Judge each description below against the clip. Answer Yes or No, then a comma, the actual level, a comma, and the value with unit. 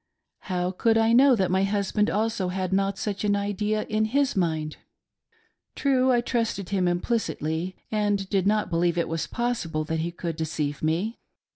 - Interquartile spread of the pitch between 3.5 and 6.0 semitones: Yes, average, 3.9 semitones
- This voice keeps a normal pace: Yes, average, 170 wpm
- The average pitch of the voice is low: No, high, 195 Hz